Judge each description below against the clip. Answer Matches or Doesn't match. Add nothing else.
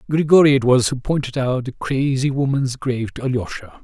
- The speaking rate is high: Doesn't match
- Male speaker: Matches